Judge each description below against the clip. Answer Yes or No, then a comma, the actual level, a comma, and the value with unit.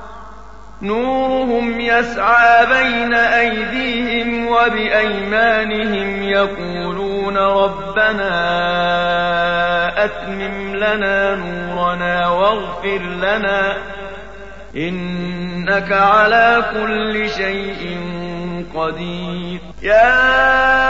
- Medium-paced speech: No, slow, 50 wpm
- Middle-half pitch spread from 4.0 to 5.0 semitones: Yes, average, 4.5 semitones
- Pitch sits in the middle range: No, high, 200 Hz